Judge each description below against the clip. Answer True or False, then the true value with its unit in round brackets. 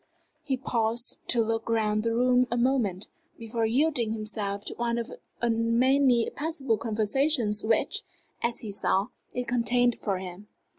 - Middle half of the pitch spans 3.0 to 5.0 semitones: False (2.4 semitones)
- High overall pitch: True (230 Hz)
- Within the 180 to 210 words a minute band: False (150 wpm)